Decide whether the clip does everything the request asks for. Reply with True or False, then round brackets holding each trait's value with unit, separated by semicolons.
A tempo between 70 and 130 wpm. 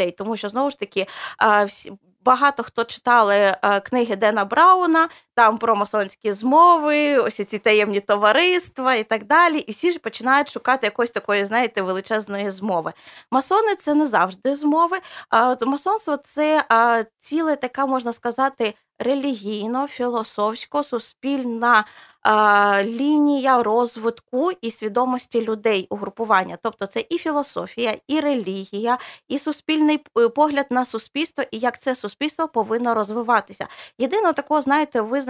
True (125 wpm)